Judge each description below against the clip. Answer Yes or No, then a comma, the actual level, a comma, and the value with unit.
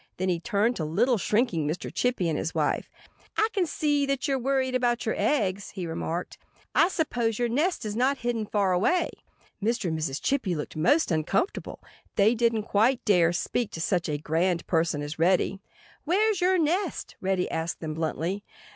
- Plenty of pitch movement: Yes, wide, 7.3 semitones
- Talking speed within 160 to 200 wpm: Yes, average, 180 wpm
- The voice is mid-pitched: No, high, 210 Hz